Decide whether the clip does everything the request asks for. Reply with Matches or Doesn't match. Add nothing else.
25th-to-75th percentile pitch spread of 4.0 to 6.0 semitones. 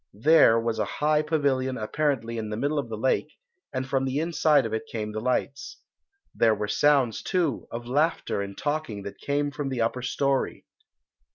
Matches